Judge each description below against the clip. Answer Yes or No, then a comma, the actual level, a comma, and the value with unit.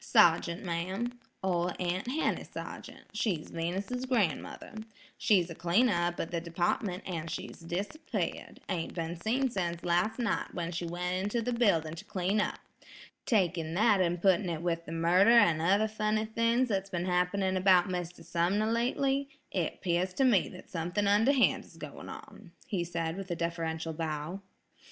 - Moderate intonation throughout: Yes, average, 4.0 semitones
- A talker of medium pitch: Yes, medium, 180 Hz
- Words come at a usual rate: Yes, average, 165 wpm